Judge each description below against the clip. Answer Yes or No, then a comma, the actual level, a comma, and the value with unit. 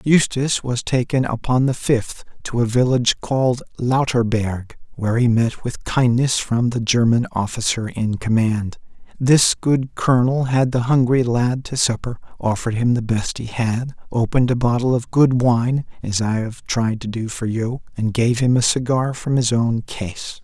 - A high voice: No, low, 120 Hz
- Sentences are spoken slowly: No, average, 175 wpm